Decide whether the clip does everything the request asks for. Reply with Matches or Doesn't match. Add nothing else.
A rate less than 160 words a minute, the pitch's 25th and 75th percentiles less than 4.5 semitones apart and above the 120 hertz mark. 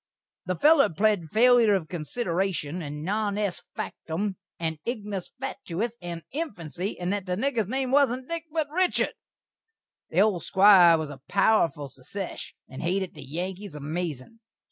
Doesn't match